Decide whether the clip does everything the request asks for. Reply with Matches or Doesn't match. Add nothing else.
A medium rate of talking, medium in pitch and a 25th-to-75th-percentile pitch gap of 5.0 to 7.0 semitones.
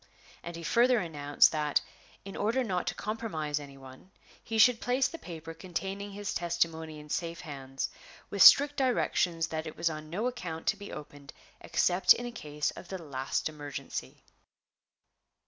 Matches